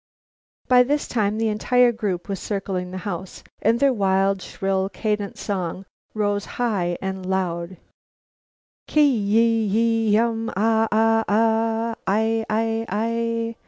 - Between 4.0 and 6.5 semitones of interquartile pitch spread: No, average, 2.8 semitones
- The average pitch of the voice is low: No, high, 215 Hz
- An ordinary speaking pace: No, slow, 130 wpm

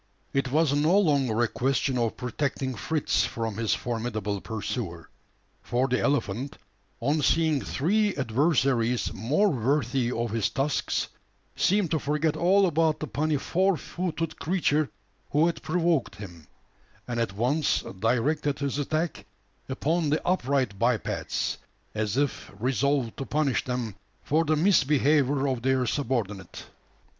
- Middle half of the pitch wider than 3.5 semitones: Yes, average, 4.7 semitones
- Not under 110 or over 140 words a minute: Yes, slow, 135 wpm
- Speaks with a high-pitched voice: No, low, 135 Hz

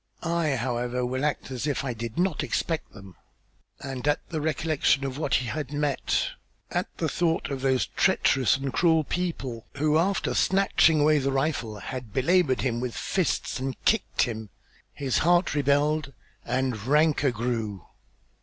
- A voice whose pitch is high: No, low, 135 Hz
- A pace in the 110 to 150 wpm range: No, average, 160 wpm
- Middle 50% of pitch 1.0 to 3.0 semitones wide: No, average, 3.8 semitones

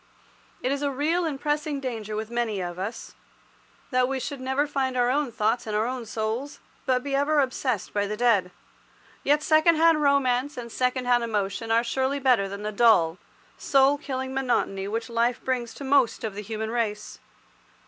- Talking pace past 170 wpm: Yes, average, 190 wpm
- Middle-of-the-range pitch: No, very high, 250 Hz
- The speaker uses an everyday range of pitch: Yes, average, 3.9 semitones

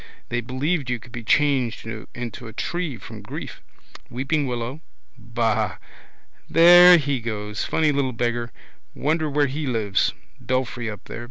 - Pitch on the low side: Yes, low, 125 Hz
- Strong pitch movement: No, average, 4.0 semitones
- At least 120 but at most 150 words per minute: Yes, average, 145 wpm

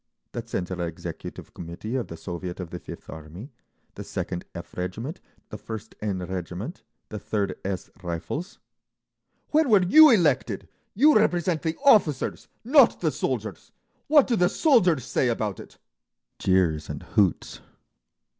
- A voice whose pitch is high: No, low, 110 Hz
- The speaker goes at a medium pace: Yes, average, 145 wpm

